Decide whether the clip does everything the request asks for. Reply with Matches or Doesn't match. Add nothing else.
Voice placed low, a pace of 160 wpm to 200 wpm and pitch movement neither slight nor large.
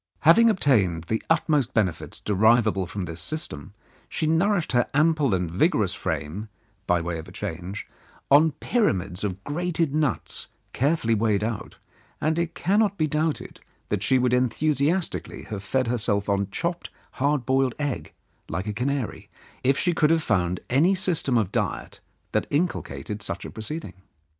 Doesn't match